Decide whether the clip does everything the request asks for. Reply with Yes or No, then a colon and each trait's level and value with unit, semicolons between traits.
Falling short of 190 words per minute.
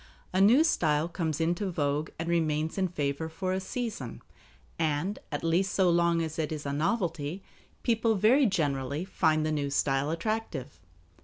Yes: average, 165 wpm